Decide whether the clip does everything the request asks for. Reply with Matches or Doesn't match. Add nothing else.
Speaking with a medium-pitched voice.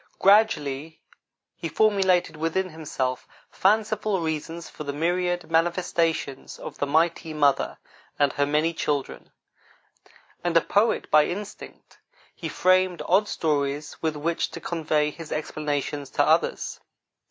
Matches